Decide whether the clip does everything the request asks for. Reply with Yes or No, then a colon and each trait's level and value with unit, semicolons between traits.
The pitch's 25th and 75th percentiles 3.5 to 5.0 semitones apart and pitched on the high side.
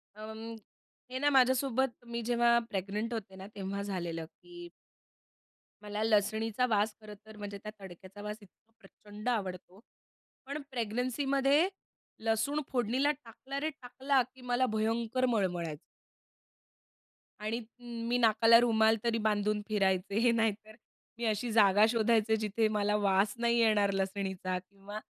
No: average, 2.9 semitones; high, 220 Hz